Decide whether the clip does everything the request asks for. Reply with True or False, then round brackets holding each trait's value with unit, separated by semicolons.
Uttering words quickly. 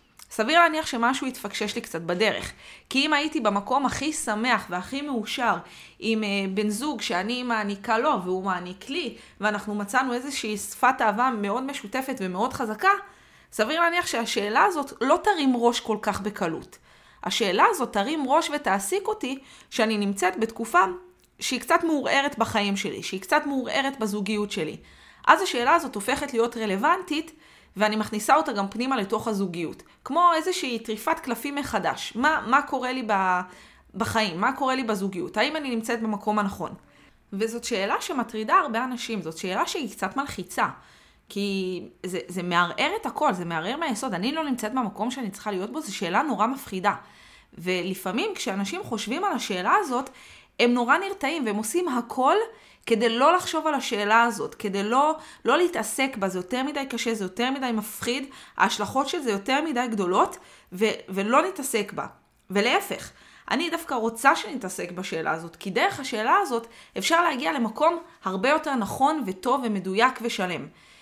True (155 wpm)